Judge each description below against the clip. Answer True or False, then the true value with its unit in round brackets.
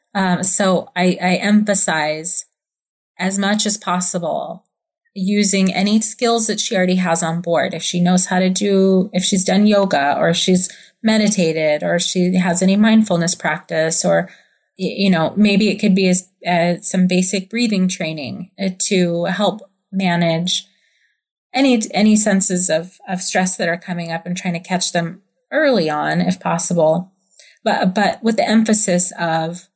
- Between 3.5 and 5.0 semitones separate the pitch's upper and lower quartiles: False (2.6 semitones)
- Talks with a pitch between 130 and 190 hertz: True (185 Hz)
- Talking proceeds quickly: False (155 wpm)